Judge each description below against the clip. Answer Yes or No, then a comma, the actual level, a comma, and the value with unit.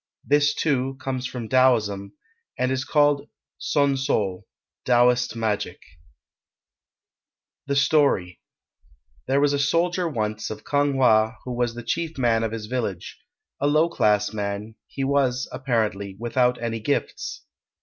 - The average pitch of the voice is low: Yes, low, 125 Hz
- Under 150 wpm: Yes, slow, 135 wpm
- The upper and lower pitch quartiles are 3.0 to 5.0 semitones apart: Yes, average, 4.3 semitones